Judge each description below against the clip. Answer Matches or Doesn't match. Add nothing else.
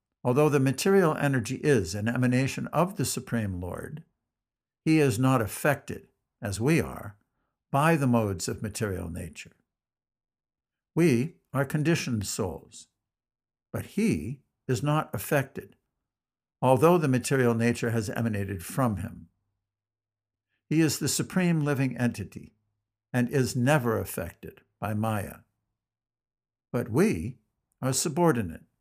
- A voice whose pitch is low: Matches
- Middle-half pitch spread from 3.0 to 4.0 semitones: Doesn't match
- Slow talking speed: Matches